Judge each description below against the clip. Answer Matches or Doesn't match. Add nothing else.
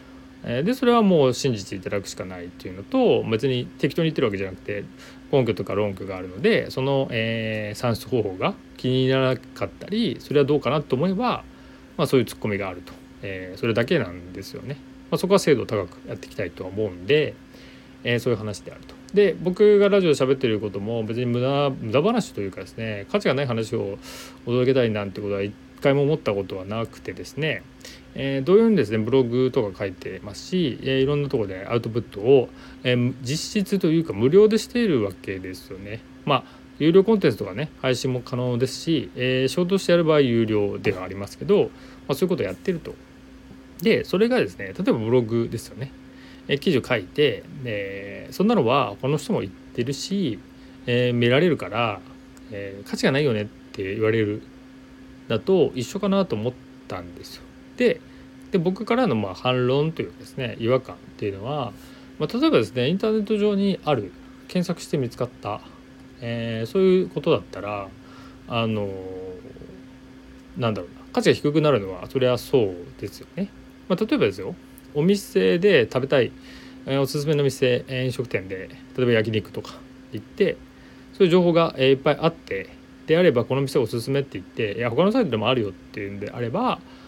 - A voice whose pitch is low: Matches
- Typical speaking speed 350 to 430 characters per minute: Matches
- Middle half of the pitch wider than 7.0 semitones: Doesn't match